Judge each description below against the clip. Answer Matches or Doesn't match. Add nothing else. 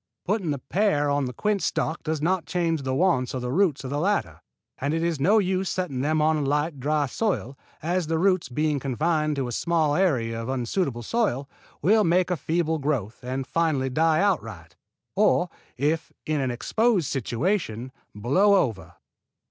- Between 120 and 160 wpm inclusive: Doesn't match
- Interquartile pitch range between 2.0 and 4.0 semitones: Doesn't match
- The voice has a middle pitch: Matches